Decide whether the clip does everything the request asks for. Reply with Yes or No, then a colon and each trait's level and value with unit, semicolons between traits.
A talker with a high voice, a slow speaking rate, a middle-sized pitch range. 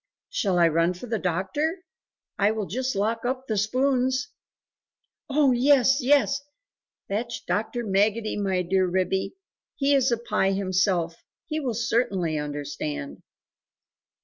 No: high, 215 Hz; slow, 130 wpm; wide, 5.7 semitones